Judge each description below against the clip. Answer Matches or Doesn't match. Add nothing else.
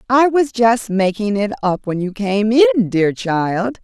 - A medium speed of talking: Matches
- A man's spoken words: Doesn't match